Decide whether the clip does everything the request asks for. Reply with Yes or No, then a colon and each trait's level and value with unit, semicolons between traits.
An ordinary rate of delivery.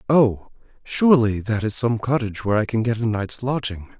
Yes: average, 195 wpm